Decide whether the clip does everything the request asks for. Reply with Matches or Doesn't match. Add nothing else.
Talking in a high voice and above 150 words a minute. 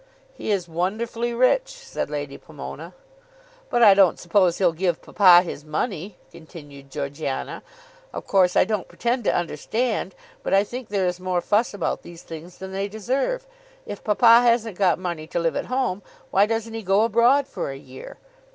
Matches